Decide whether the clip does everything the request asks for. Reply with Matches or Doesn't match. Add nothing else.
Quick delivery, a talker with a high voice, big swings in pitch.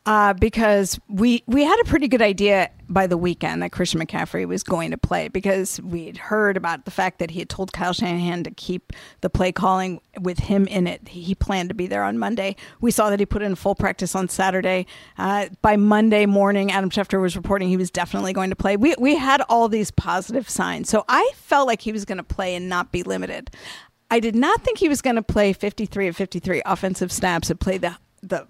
Doesn't match